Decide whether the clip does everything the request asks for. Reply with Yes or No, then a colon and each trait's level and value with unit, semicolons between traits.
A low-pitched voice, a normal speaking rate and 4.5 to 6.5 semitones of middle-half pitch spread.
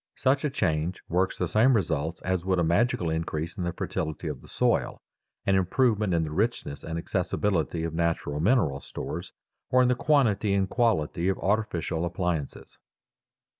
Yes: very low, 90 Hz; average, 170 wpm; average, 4.8 semitones